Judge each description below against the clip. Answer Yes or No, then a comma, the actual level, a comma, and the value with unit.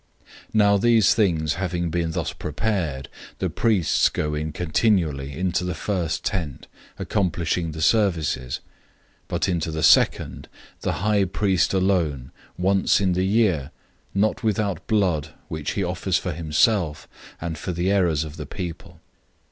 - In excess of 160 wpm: No, average, 150 wpm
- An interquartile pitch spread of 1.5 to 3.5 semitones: No, average, 4.0 semitones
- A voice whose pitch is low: Yes, very low, 90 Hz